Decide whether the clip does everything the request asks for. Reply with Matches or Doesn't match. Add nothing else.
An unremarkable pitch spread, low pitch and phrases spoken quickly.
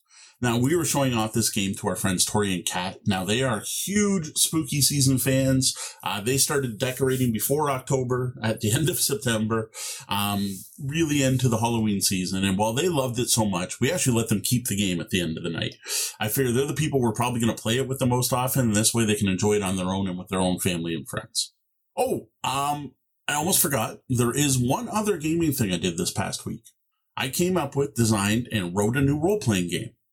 Matches